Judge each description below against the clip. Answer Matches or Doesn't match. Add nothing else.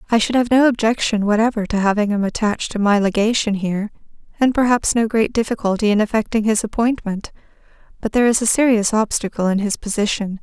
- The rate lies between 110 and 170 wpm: Doesn't match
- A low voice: Doesn't match